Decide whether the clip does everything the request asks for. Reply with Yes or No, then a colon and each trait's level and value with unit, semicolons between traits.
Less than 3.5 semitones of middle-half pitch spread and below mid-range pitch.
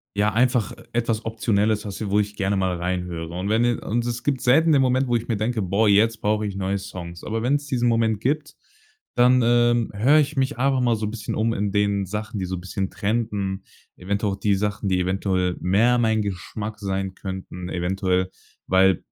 No: average, 3.8 semitones; low, 105 Hz